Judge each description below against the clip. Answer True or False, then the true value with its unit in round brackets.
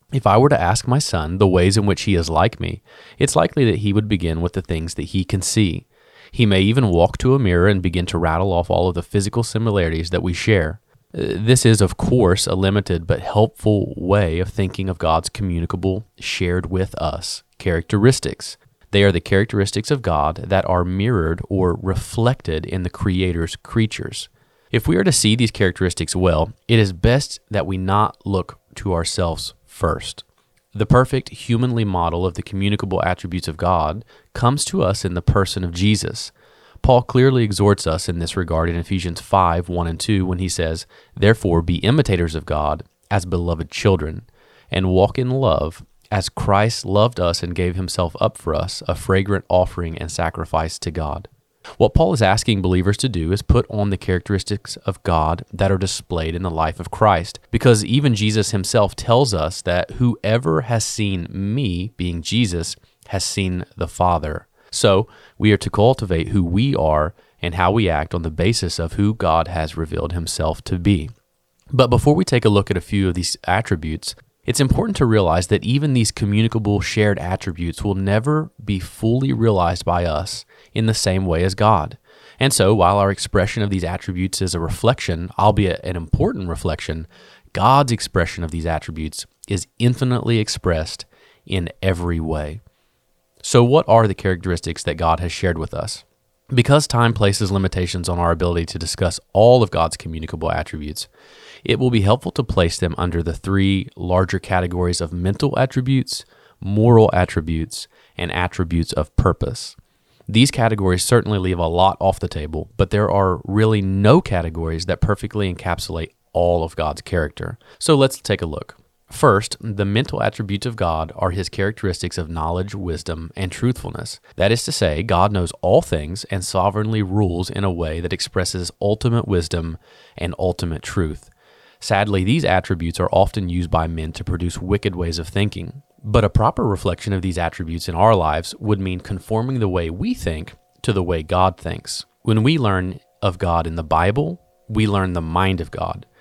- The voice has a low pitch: True (95 Hz)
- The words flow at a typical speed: True (180 wpm)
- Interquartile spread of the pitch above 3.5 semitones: True (3.9 semitones)